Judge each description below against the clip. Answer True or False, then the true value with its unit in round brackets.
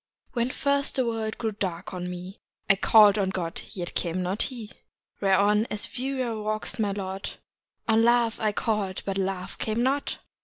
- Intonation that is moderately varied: True (3.3 semitones)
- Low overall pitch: False (210 Hz)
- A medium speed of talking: True (175 wpm)